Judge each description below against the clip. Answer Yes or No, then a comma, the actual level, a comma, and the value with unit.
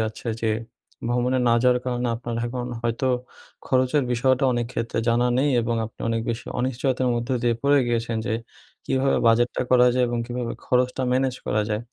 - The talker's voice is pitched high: No, low, 120 Hz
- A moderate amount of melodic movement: No, narrow, 1.7 semitones